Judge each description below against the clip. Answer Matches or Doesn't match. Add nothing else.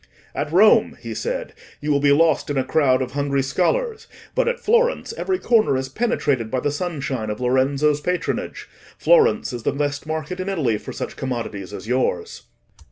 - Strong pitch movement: Matches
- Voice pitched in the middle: Matches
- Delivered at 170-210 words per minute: Matches